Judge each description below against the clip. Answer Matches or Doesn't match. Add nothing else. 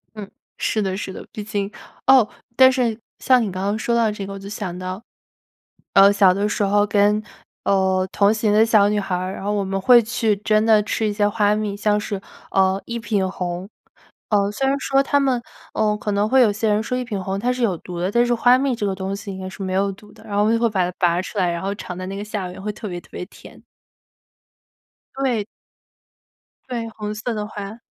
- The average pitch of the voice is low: Doesn't match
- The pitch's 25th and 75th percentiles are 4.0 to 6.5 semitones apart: Doesn't match